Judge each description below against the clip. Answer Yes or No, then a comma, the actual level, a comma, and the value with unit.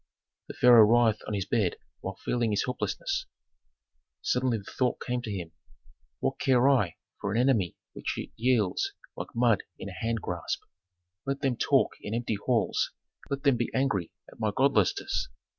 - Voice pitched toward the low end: Yes, low, 115 Hz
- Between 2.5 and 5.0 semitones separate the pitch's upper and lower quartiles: Yes, average, 3.7 semitones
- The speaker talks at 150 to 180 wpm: Yes, average, 165 wpm